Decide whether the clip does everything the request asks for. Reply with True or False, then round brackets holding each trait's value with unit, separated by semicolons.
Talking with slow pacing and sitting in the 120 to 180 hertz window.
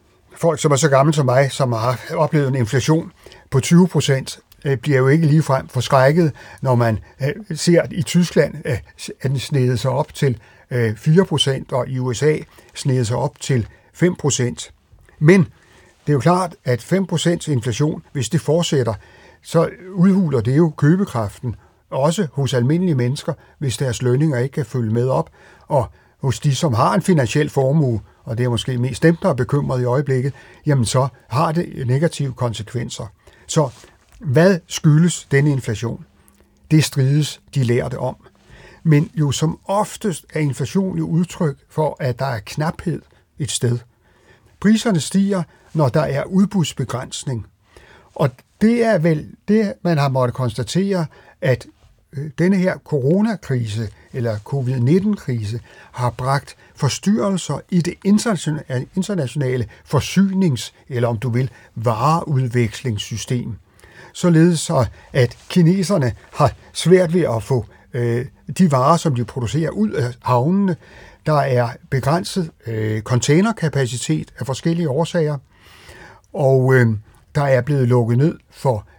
True (135 wpm; 135 Hz)